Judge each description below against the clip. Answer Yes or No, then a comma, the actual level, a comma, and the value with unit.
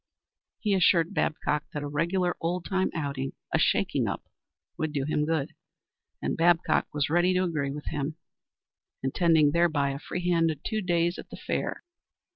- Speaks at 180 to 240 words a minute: No, average, 165 wpm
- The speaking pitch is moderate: Yes, medium, 165 Hz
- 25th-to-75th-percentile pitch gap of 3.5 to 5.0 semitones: No, average, 3.1 semitones